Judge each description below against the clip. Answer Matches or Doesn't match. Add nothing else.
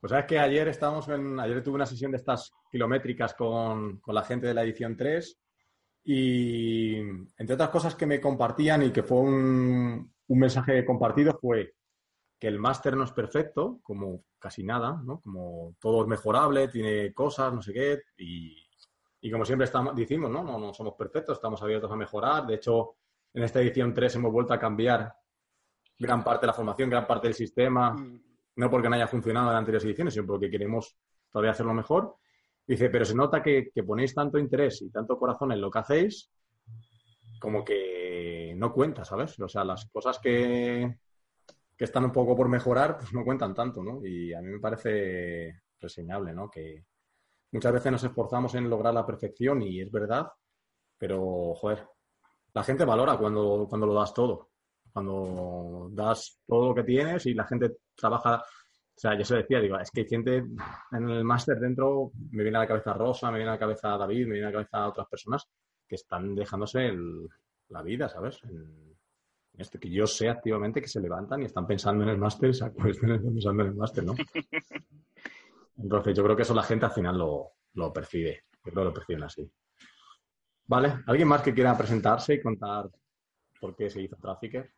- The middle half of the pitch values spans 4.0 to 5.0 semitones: Doesn't match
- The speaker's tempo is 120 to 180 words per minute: Doesn't match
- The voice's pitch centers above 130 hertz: Doesn't match